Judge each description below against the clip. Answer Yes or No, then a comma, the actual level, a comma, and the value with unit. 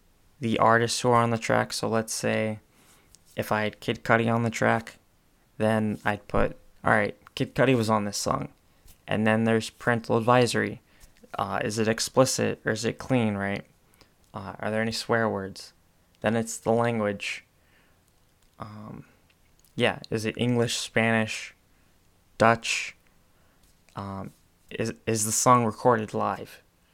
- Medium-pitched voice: No, low, 110 Hz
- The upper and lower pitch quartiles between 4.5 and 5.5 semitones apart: No, average, 3.3 semitones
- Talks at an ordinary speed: Yes, average, 145 wpm